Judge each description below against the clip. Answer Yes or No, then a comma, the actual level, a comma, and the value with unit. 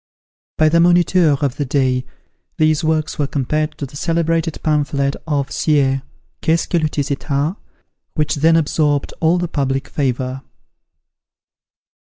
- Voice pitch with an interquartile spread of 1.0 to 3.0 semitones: Yes, narrow, 2.5 semitones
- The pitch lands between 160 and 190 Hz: No, medium, 150 Hz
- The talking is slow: No, average, 145 wpm